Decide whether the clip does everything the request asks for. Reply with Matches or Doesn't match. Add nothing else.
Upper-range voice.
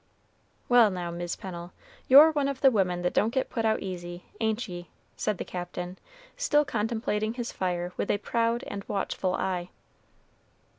Matches